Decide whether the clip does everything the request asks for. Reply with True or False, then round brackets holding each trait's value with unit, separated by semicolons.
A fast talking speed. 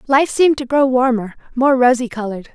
False (190 wpm)